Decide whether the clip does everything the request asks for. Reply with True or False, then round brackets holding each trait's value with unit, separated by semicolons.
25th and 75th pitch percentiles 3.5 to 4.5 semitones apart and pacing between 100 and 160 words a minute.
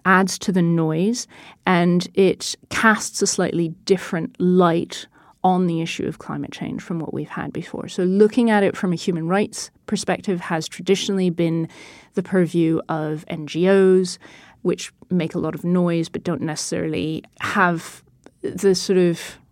False (2.6 semitones; 155 wpm)